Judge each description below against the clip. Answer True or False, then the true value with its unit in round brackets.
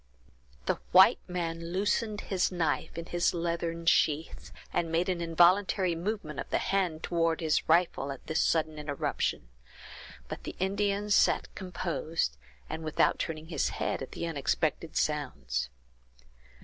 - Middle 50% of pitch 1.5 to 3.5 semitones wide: True (2.4 semitones)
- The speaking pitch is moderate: True (165 Hz)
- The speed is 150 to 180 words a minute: False (140 wpm)